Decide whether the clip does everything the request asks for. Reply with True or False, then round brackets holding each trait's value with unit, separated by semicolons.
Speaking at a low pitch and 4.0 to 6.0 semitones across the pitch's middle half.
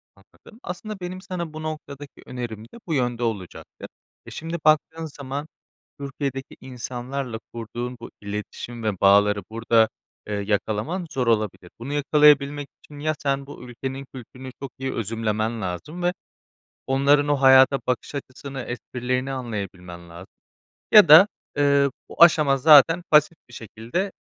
True (130 Hz; 4.4 semitones)